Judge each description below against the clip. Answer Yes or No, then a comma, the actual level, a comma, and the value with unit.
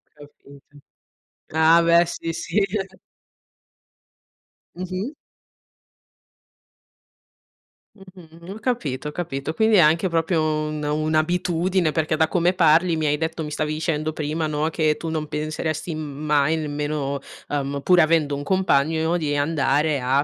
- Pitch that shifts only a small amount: Yes, narrow, 2.1 semitones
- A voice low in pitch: No, medium, 155 Hz